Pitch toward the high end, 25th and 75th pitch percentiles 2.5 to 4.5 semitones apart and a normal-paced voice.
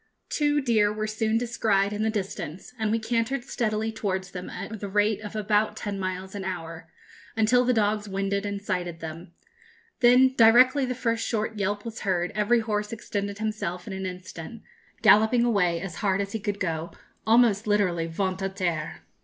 Yes: high, 210 Hz; average, 2.9 semitones; average, 180 wpm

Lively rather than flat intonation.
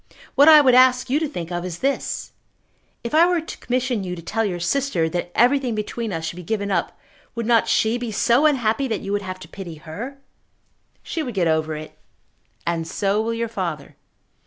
Yes: wide, 6.4 semitones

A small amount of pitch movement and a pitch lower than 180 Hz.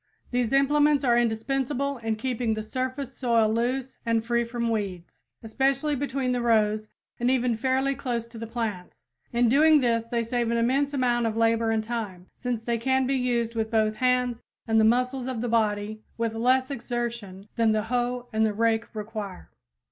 No: narrow, 2.3 semitones; high, 235 Hz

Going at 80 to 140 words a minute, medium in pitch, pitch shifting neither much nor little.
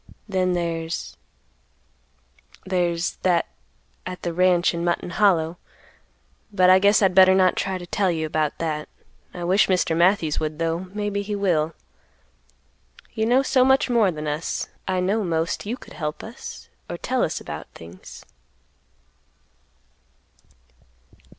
Yes: slow, 135 wpm; medium, 180 Hz; average, 3.0 semitones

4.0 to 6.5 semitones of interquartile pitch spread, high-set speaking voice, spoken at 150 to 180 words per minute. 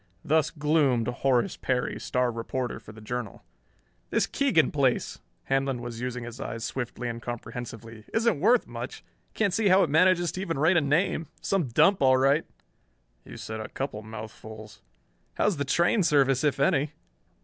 No: average, 5.2 semitones; low, 135 Hz; average, 165 wpm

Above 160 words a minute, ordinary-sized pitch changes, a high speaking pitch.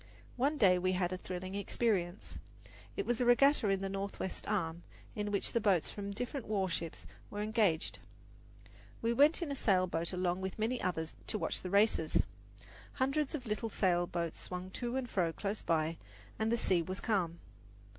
Yes: average, 185 wpm; average, 4.3 semitones; high, 200 Hz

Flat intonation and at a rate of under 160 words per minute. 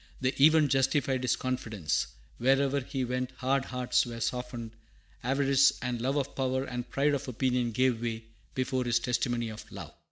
No: narrow, 1.8 semitones; average, 165 wpm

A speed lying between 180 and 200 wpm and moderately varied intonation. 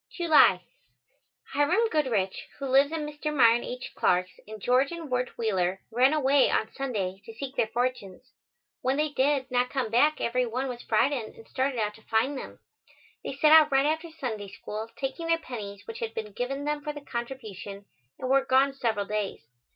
Yes: average, 190 wpm; average, 4.4 semitones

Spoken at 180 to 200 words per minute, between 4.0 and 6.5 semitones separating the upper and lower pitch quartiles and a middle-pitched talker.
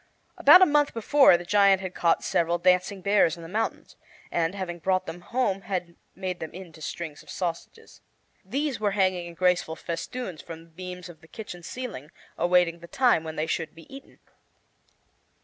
No: average, 185 wpm; average, 3.1 semitones; medium, 180 Hz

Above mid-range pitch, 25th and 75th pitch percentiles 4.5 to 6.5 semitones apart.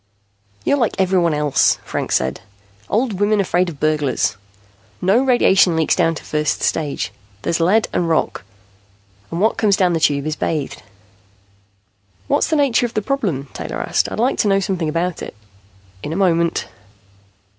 No: medium, 175 Hz; average, 5.2 semitones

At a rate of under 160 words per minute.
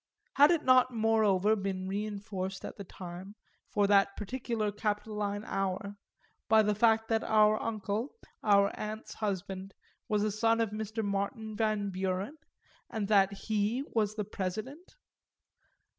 Yes: average, 140 wpm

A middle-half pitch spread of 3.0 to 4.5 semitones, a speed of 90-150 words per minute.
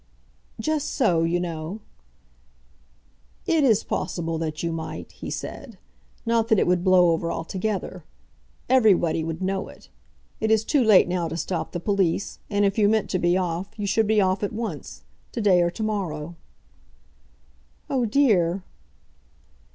No: average, 4.2 semitones; average, 160 wpm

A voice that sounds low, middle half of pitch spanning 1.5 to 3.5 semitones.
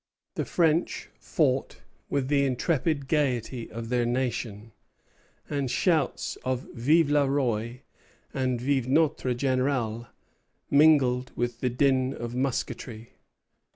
Yes: low, 130 Hz; average, 2.8 semitones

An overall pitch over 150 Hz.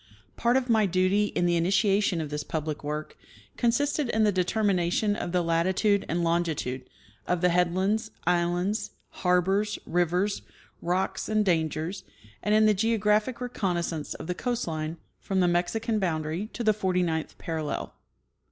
Yes: medium, 185 Hz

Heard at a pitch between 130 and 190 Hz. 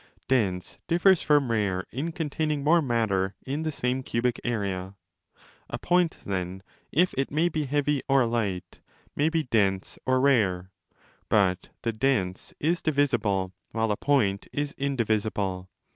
No: low, 120 Hz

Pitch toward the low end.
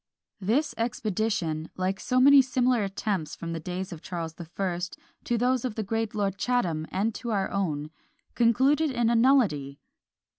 No: high, 205 Hz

